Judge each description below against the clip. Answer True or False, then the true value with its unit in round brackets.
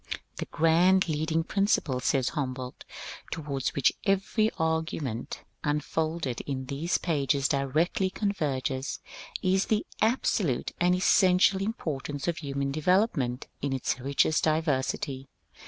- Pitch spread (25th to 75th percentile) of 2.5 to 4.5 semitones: False (4.9 semitones)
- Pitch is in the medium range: True (155 Hz)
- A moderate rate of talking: False (115 wpm)